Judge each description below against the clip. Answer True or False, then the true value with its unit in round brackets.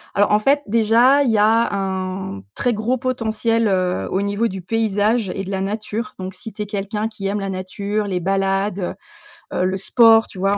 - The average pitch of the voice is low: False (205 Hz)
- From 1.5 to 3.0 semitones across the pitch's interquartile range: True (2.7 semitones)